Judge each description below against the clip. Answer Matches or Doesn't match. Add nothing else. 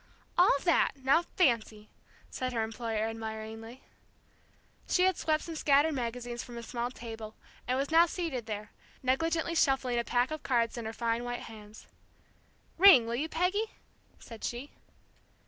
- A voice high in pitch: Matches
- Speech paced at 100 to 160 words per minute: Matches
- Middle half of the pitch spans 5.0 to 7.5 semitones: Matches